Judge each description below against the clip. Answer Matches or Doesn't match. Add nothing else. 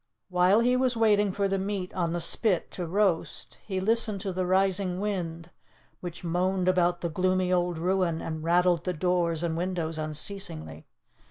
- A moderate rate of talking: Matches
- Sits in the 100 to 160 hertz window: Doesn't match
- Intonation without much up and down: Matches